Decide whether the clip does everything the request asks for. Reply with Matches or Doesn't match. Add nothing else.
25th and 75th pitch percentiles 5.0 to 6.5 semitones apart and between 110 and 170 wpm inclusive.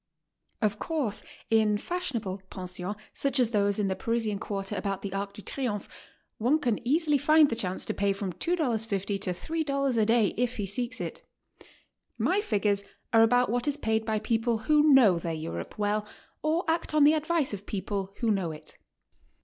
Doesn't match